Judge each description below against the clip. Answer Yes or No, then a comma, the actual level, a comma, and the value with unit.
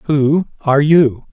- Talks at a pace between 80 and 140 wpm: Yes, slow, 135 wpm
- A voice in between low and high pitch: Yes, medium, 145 Hz